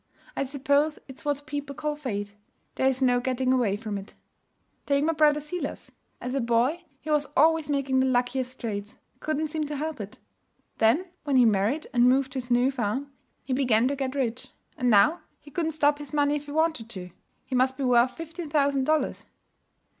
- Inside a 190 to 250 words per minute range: Yes, average, 195 wpm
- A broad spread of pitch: No, average, 3.2 semitones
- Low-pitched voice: No, very high, 270 Hz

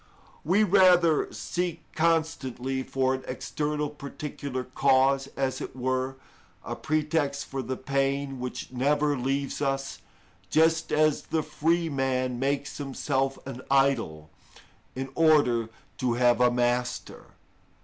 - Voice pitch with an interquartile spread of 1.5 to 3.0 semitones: Yes, average, 2.7 semitones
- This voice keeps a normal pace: No, slow, 120 wpm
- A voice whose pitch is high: No, low, 135 Hz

